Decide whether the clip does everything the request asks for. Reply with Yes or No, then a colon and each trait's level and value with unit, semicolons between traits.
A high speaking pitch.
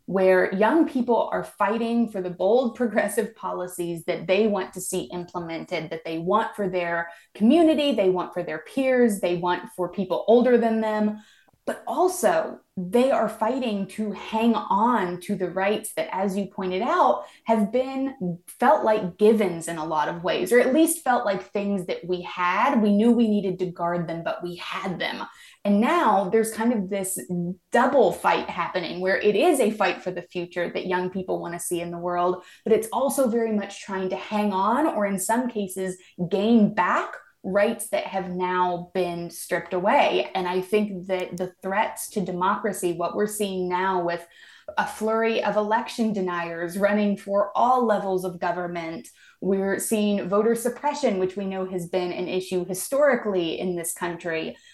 Yes: high, 195 Hz